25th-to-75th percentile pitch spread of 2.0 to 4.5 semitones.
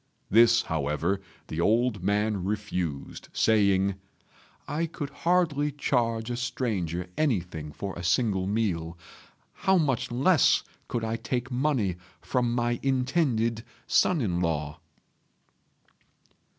No: wide, 5.6 semitones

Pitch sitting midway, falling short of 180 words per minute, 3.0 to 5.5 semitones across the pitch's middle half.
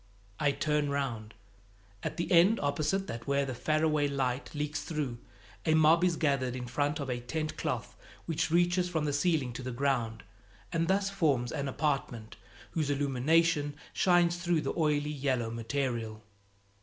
Yes: medium, 145 Hz; average, 160 wpm; average, 4.0 semitones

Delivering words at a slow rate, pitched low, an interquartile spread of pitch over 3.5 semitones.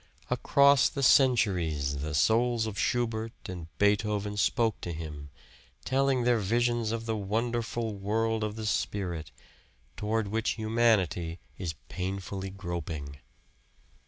Yes: slow, 120 wpm; low, 105 Hz; average, 4.2 semitones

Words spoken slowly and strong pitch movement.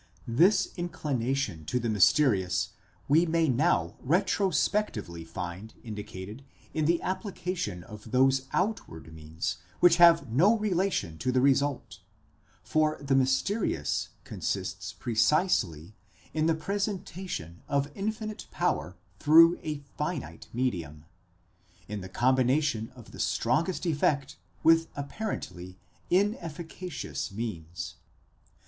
Yes: slow, 110 wpm; wide, 8.5 semitones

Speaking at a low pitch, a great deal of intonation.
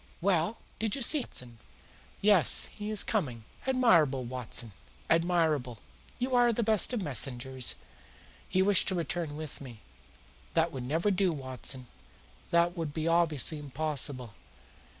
No: medium, 160 Hz; wide, 7.0 semitones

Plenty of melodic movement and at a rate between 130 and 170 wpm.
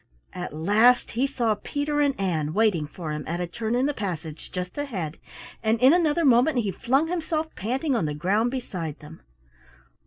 No: wide, 7.9 semitones; average, 185 wpm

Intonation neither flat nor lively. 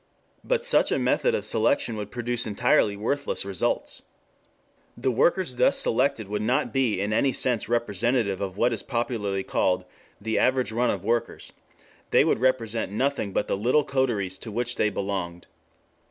Yes: average, 4.1 semitones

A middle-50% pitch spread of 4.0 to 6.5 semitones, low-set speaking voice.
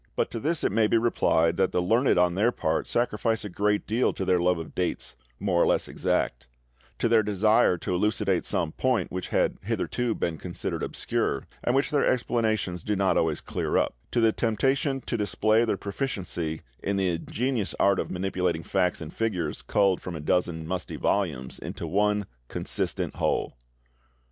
Yes: average, 4.3 semitones; low, 100 Hz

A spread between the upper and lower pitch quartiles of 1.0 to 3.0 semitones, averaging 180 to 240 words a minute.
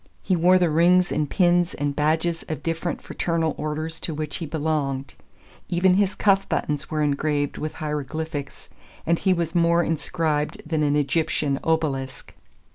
No: narrow, 2.4 semitones; average, 155 wpm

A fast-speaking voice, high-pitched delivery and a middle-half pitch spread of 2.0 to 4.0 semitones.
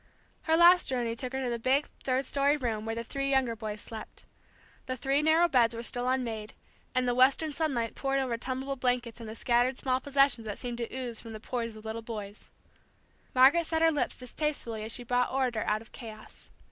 Yes: fast, 210 wpm; very high, 250 Hz; average, 2.9 semitones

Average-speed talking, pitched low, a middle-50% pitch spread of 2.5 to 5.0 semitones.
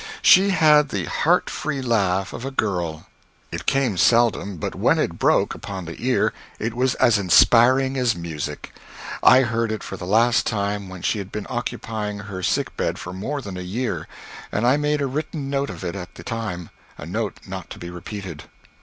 No: average, 195 wpm; low, 110 Hz; wide, 5.6 semitones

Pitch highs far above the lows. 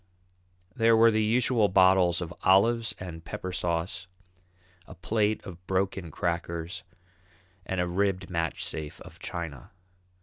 No: average, 3.3 semitones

